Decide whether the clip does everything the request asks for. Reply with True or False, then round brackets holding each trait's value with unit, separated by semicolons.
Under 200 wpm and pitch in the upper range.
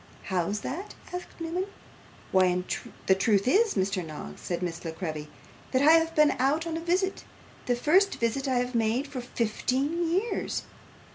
True (165 wpm; 255 Hz)